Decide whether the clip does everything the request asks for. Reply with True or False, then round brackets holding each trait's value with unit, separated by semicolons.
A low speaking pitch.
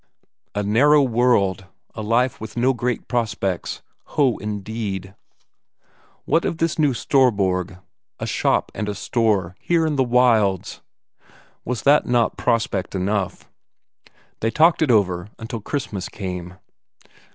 True (110 Hz)